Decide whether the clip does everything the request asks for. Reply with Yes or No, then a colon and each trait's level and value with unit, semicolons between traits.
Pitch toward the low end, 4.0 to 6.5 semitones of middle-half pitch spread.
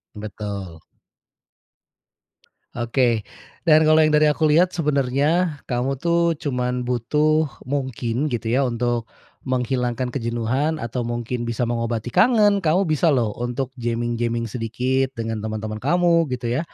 Yes: low, 125 Hz; average, 4.4 semitones